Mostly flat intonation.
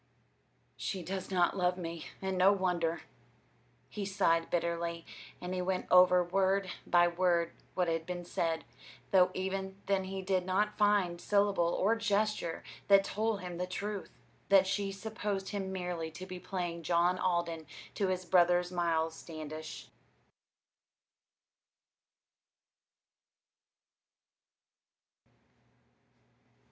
Yes: narrow, 2.1 semitones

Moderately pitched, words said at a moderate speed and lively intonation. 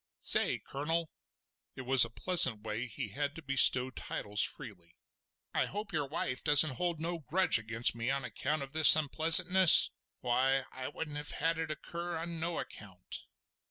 No: medium, 145 Hz; average, 160 wpm; average, 4.6 semitones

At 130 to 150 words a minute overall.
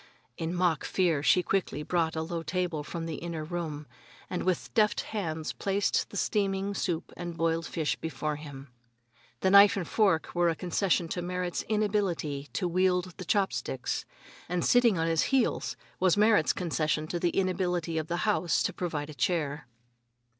No: average, 170 wpm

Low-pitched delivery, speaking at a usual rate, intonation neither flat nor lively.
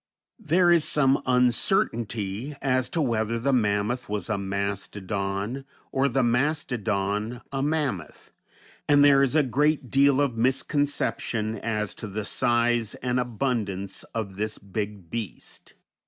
No: low, 120 Hz; slow, 130 wpm; average, 4.7 semitones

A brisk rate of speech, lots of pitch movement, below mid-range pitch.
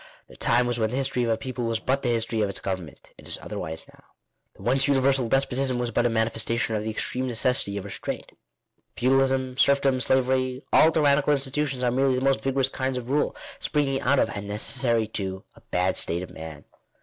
No: fast, 215 wpm; average, 3.3 semitones; low, 125 Hz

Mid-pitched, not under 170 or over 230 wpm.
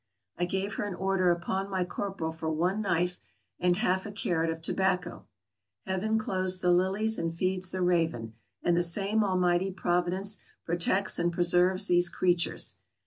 No: medium, 180 Hz; average, 160 wpm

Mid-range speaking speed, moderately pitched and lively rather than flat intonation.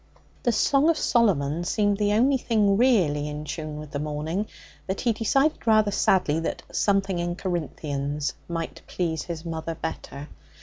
Yes: average, 160 wpm; medium, 175 Hz; wide, 5.8 semitones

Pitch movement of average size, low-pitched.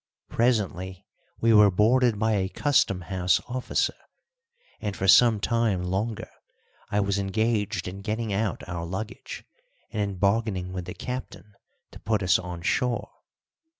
Yes: average, 3.3 semitones; low, 105 Hz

